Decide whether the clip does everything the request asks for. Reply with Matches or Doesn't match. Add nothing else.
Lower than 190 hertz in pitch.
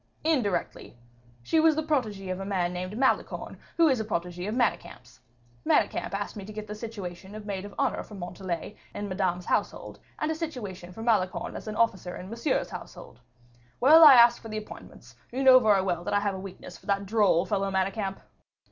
Doesn't match